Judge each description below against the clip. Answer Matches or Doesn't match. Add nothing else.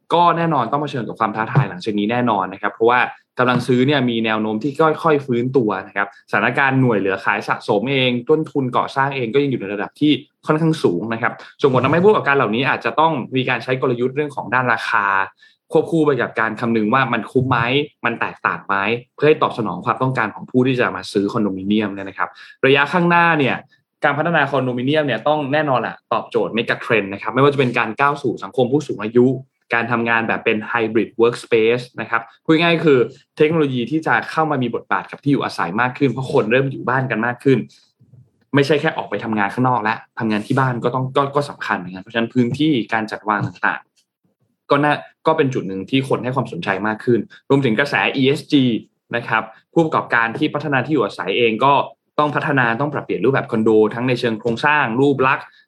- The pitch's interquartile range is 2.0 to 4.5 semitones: Matches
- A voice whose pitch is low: Matches